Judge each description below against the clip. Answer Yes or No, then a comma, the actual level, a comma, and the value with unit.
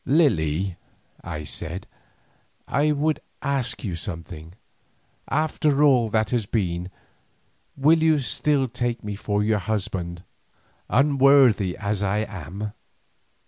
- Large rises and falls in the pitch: Yes, wide, 7.1 semitones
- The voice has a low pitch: Yes, low, 110 Hz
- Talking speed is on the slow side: Yes, slow, 110 wpm